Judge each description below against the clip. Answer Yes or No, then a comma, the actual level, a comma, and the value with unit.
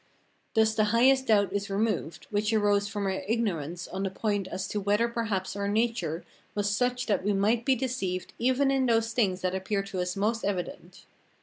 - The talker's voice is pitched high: Yes, high, 205 Hz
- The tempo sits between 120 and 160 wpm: No, average, 200 wpm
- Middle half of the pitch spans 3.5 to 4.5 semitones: No, average, 3.0 semitones